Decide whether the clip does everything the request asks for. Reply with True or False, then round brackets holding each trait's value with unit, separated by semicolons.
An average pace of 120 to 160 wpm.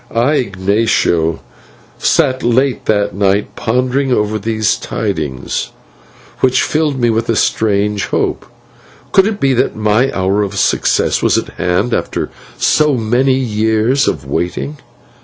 True (135 wpm)